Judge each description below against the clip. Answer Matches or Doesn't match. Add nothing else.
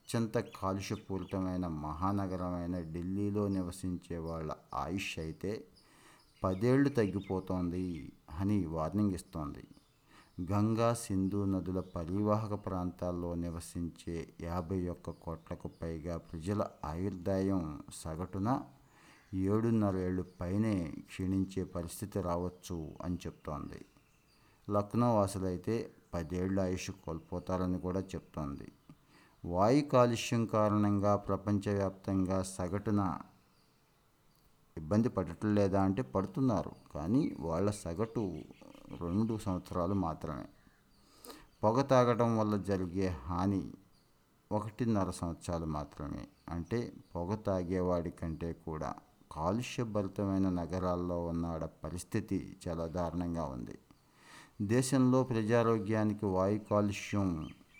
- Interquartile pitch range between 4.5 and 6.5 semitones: Doesn't match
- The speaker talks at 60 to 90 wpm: Matches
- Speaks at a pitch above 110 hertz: Doesn't match